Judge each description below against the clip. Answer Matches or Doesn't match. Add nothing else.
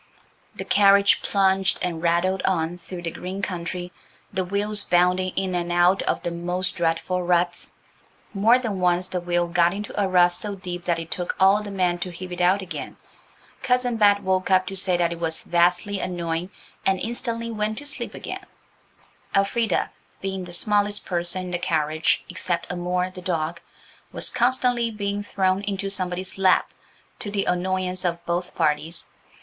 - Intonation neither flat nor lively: Doesn't match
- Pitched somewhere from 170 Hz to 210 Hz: Matches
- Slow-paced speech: Doesn't match